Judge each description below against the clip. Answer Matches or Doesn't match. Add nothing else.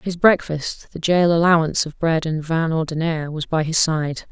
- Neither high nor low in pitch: Matches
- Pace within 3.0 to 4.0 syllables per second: Doesn't match